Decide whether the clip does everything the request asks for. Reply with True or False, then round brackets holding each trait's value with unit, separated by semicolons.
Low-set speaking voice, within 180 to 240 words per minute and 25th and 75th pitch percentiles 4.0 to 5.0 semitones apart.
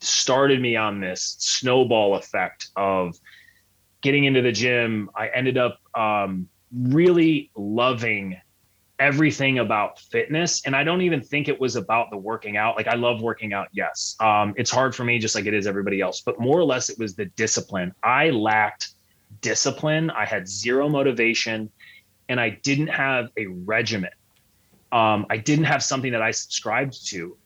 False (115 Hz; 170 wpm; 4.4 semitones)